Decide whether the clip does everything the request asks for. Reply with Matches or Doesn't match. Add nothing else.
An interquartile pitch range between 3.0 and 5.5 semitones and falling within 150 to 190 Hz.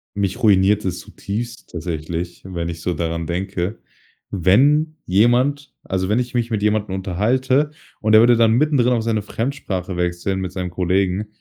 Doesn't match